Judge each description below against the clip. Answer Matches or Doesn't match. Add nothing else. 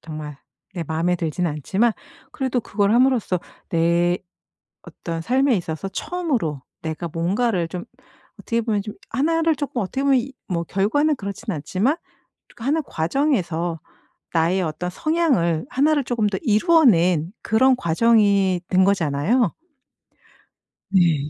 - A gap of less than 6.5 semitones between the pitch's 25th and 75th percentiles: Doesn't match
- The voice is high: Matches